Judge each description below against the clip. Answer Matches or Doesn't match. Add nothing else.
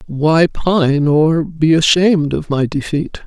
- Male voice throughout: Doesn't match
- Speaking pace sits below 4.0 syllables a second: Matches